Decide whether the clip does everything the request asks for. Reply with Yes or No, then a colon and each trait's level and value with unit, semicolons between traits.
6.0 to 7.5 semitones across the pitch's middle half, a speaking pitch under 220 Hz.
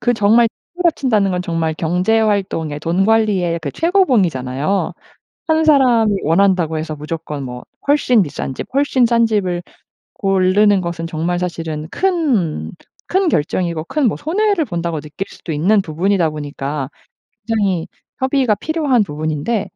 Yes: wide, 6.7 semitones; high, 190 Hz